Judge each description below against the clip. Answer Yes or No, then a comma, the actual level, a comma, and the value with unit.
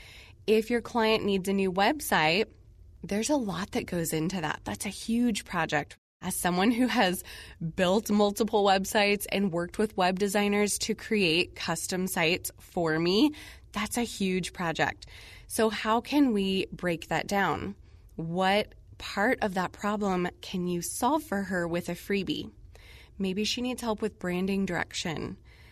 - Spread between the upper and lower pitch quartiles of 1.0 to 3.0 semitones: No, average, 3.7 semitones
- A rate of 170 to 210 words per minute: No, average, 155 wpm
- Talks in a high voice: Yes, high, 195 Hz